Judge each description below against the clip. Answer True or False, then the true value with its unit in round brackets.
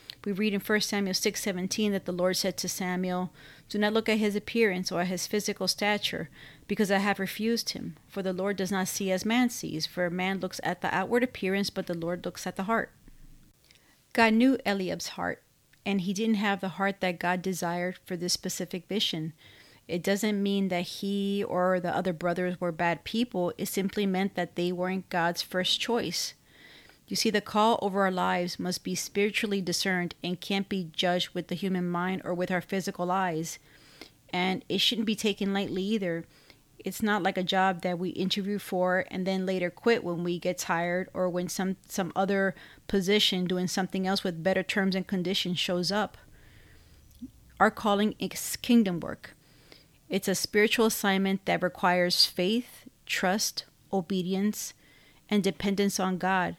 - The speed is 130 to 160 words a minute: False (180 wpm)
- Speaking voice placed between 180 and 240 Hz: True (190 Hz)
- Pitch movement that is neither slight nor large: False (2.2 semitones)